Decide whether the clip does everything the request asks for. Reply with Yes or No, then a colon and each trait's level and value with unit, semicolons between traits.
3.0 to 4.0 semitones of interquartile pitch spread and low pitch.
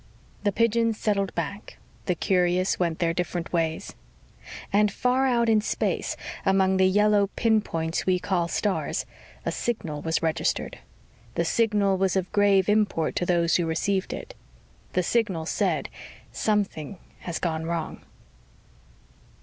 No: average, 3.6 semitones; high, 190 Hz